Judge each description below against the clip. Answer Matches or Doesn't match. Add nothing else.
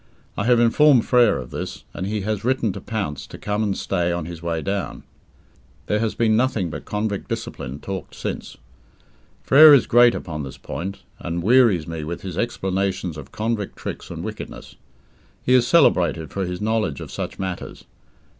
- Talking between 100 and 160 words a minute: Doesn't match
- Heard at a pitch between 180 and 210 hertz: Doesn't match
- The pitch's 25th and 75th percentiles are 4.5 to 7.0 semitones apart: Matches